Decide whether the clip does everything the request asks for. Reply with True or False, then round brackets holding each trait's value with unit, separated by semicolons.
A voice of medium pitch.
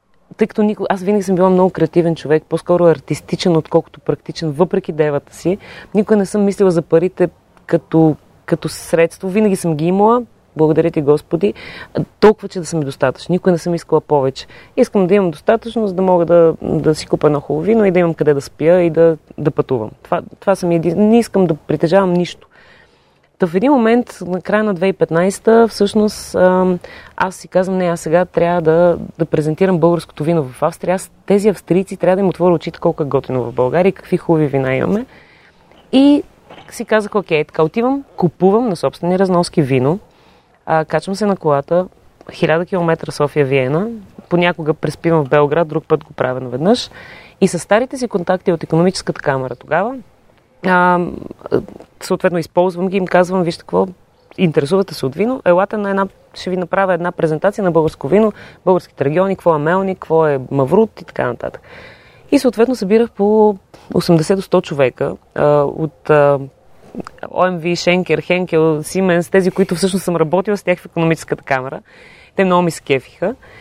True (175 Hz)